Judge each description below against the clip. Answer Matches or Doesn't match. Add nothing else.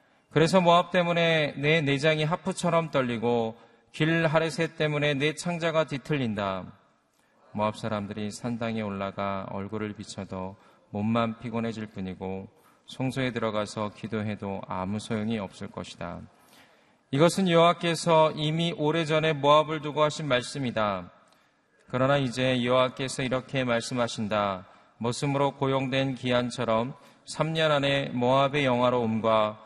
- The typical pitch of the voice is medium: Doesn't match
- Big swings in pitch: Matches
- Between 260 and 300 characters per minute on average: Matches